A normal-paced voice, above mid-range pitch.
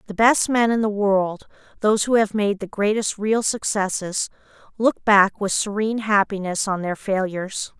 Yes: average, 170 wpm; high, 205 Hz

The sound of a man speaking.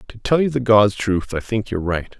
Yes: male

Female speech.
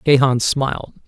No: male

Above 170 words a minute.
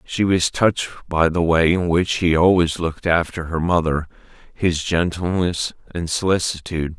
No: average, 155 wpm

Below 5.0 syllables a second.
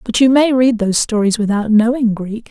No: 5.4 syllables/s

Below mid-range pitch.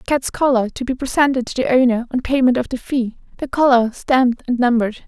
No: very high, 250 Hz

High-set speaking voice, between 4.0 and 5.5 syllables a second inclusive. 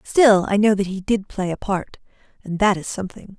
Yes: high, 200 Hz; 5.2 syllables/s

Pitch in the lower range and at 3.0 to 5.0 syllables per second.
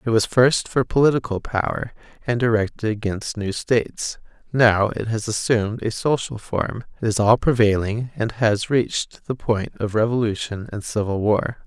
Yes: low, 110 Hz; 4.6 syllables/s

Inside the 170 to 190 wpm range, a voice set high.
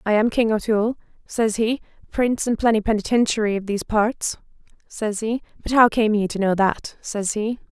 Yes: average, 180 wpm; high, 220 Hz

